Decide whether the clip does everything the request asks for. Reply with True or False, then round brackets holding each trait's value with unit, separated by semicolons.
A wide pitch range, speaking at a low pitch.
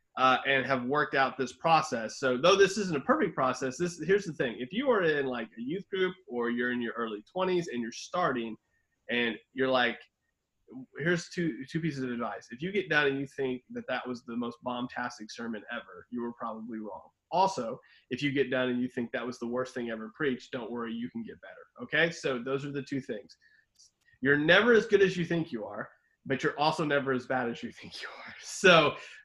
False (4.9 semitones; 130 Hz)